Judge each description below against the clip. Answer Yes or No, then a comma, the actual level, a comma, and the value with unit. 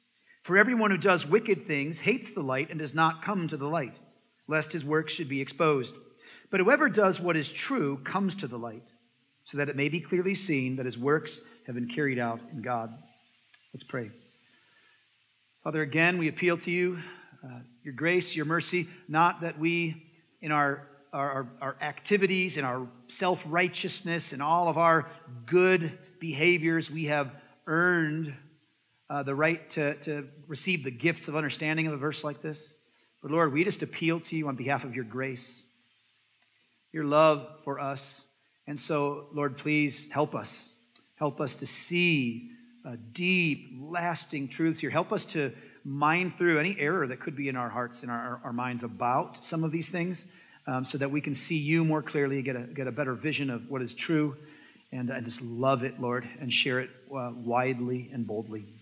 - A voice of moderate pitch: Yes, medium, 150 Hz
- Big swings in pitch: No, average, 3.9 semitones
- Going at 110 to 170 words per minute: No, average, 185 wpm